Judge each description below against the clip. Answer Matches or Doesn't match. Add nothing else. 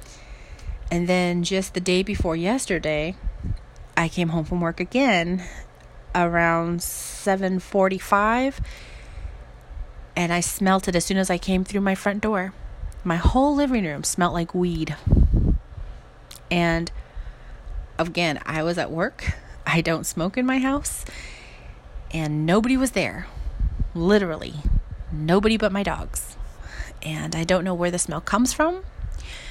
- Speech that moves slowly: Matches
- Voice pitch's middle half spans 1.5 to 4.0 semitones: Matches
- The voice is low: Doesn't match